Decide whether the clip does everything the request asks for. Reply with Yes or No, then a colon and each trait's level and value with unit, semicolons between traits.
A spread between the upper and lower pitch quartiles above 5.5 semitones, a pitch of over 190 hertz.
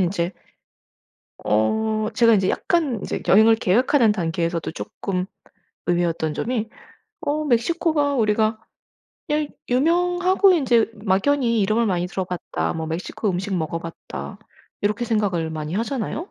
Yes: wide, 6.2 semitones; high, 215 Hz